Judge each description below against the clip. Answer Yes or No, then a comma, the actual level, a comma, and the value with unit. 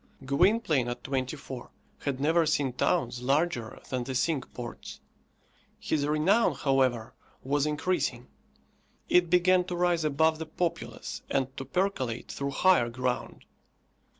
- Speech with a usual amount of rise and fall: Yes, average, 4.7 semitones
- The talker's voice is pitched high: No, medium, 140 Hz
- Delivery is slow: Yes, slow, 130 wpm